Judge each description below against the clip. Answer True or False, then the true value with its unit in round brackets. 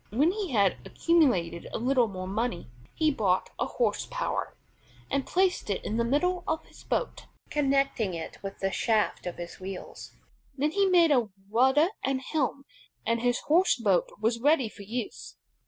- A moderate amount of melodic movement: False (6.9 semitones)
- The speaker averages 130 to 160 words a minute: False (170 wpm)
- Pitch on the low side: False (250 Hz)